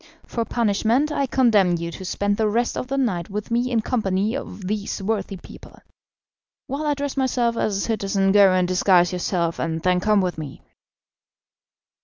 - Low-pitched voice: No, high, 205 Hz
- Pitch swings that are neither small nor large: Yes, average, 4.4 semitones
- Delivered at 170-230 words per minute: Yes, average, 180 wpm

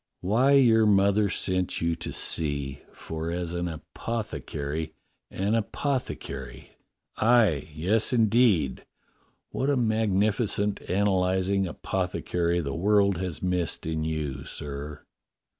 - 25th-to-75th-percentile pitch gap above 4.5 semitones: Yes, average, 5.0 semitones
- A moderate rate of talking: No, slow, 125 wpm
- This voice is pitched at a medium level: No, very low, 95 Hz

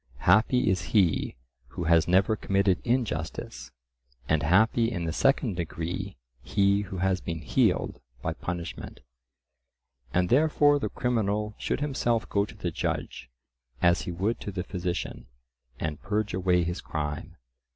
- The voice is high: No, very low, 95 Hz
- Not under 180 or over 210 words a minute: No, average, 140 wpm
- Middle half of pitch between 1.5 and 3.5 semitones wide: No, average, 3.9 semitones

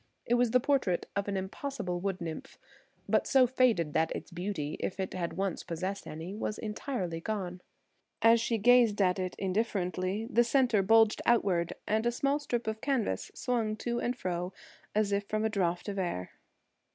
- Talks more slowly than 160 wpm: No, average, 175 wpm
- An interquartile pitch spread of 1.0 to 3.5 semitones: No, average, 4.4 semitones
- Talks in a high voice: Yes, high, 205 Hz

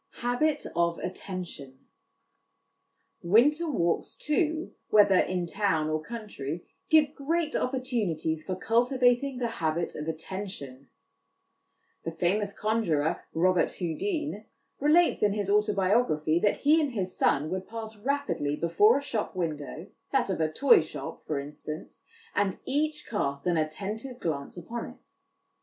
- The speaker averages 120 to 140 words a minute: Yes, slow, 135 wpm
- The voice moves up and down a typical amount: No, wide, 7.4 semitones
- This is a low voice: No, high, 200 Hz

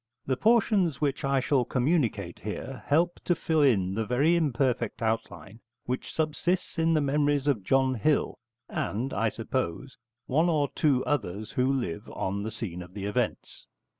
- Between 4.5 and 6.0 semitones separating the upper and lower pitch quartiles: Yes, average, 5.2 semitones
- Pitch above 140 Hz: No, low, 130 Hz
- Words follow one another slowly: No, average, 165 wpm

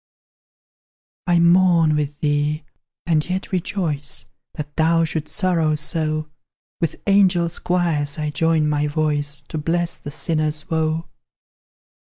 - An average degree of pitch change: No, narrow, 2.1 semitones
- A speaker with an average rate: No, slow, 120 wpm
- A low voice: No, medium, 155 Hz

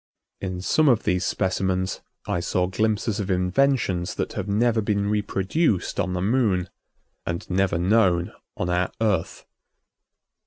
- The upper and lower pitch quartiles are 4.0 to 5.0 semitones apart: No, average, 3.0 semitones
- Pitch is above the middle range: No, very low, 95 Hz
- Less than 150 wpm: Yes, average, 140 wpm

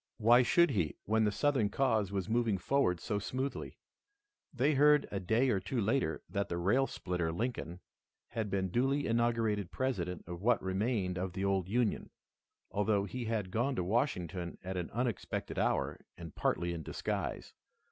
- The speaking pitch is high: No, low, 105 Hz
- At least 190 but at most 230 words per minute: No, average, 170 wpm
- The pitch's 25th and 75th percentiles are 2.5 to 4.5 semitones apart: No, average, 4.9 semitones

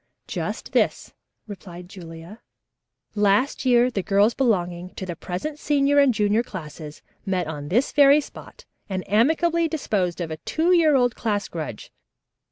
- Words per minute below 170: Yes, average, 150 wpm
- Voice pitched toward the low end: No, high, 205 Hz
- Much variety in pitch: Yes, wide, 7.5 semitones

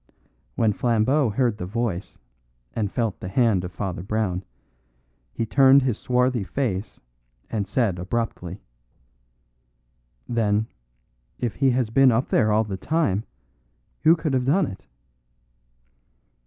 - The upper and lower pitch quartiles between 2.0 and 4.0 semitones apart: No, average, 4.4 semitones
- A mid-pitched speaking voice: No, low, 115 Hz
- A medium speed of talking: No, slow, 130 wpm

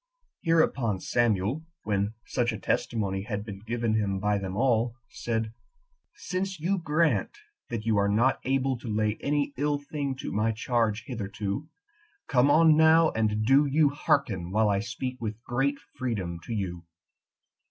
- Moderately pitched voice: No, low, 115 Hz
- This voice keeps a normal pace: Yes, average, 160 wpm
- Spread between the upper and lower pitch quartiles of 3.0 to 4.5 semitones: No, average, 5.1 semitones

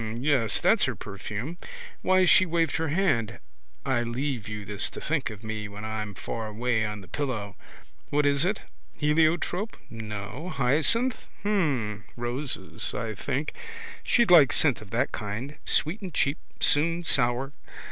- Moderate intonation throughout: No, wide, 6.5 semitones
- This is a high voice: No, low, 130 Hz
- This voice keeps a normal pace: Yes, average, 150 wpm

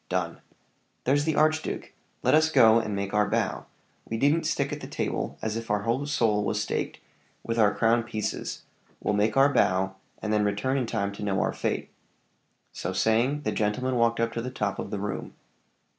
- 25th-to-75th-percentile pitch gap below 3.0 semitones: No, average, 3.7 semitones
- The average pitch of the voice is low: Yes, low, 115 Hz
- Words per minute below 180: No, average, 200 wpm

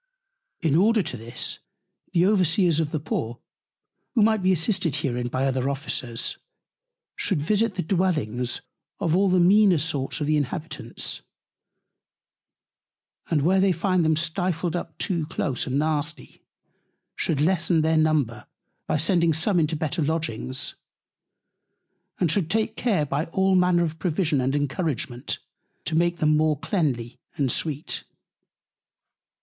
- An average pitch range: Yes, average, 4.0 semitones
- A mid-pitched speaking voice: Yes, medium, 160 Hz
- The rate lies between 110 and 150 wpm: Yes, average, 140 wpm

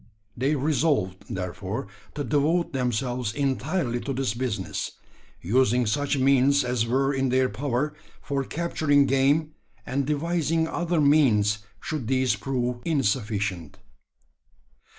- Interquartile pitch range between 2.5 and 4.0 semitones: Yes, average, 3.3 semitones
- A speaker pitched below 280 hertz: Yes, low, 135 Hz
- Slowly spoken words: Yes, slow, 115 wpm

